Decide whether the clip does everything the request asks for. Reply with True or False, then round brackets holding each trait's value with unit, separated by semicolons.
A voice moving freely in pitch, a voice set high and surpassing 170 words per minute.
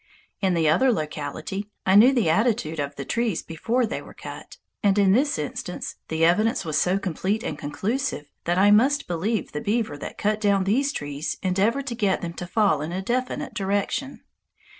True (5.8 semitones; 200 Hz; 190 wpm)